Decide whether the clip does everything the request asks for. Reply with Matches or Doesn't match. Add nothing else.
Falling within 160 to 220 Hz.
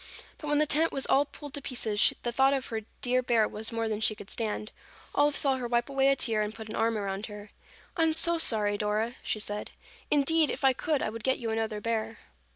Doesn't match